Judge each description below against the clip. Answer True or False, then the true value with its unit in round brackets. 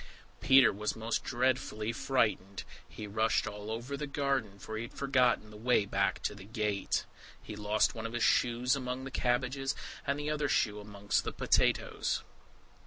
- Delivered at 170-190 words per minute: True (175 wpm)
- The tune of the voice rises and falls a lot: False (3.9 semitones)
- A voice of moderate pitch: False (115 Hz)